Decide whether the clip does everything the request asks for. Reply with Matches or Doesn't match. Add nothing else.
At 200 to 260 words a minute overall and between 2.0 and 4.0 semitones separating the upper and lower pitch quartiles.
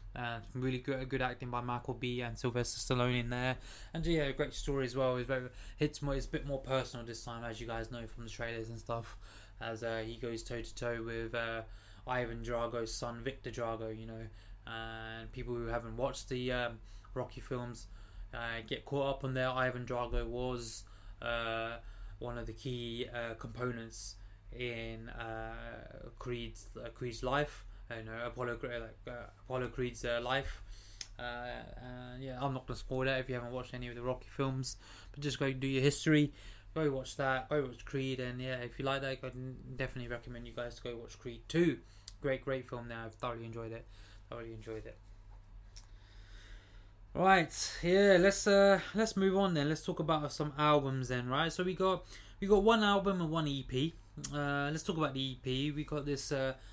Matches